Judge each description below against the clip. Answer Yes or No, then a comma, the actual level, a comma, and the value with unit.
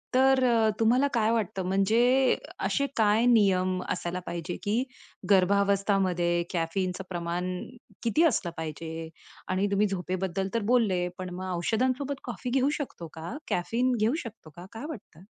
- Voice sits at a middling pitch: No, high, 200 Hz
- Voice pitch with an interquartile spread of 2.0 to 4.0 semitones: No, average, 4.6 semitones